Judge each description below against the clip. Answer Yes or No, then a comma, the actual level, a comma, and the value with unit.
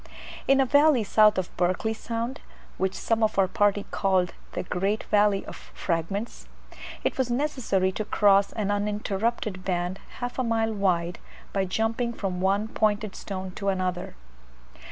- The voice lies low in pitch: No, high, 205 Hz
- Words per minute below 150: No, average, 155 wpm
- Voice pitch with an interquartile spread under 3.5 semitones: Yes, average, 3.0 semitones